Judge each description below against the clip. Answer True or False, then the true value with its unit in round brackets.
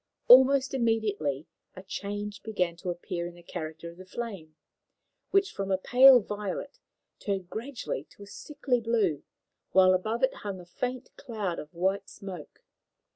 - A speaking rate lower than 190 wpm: True (155 wpm)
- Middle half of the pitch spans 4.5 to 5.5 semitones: True (4.9 semitones)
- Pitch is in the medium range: False (200 Hz)